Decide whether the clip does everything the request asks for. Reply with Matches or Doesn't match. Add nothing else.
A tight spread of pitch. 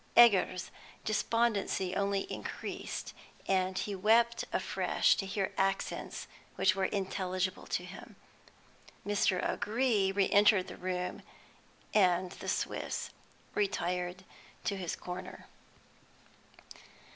Matches